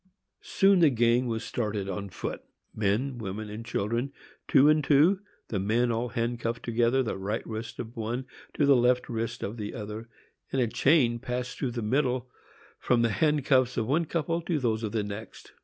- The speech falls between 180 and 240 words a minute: Yes, average, 185 wpm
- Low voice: Yes, low, 120 Hz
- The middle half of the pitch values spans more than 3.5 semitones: No, average, 3.1 semitones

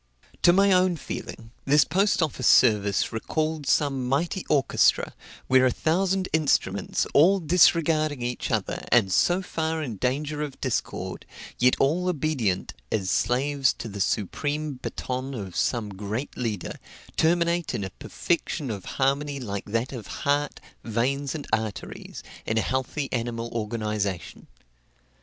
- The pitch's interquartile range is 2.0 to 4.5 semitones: No, wide, 5.5 semitones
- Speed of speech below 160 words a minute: Yes, average, 140 wpm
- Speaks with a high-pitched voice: No, low, 135 Hz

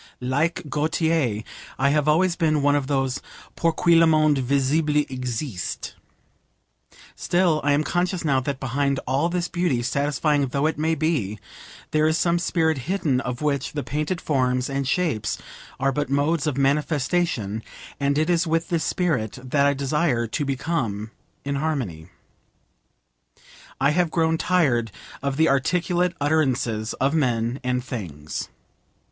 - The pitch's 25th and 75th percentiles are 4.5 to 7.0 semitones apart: No, average, 3.7 semitones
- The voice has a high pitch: No, medium, 145 Hz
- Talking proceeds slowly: No, average, 150 wpm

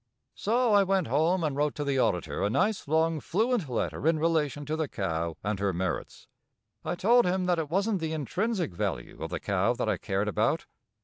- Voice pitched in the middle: Yes, medium, 160 Hz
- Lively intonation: Yes, wide, 8.3 semitones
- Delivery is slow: No, fast, 205 wpm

